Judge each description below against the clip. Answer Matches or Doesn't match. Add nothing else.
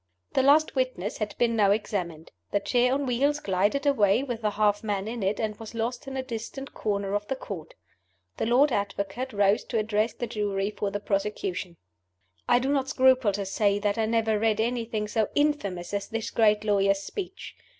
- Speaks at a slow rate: Doesn't match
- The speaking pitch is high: Matches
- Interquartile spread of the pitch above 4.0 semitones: Doesn't match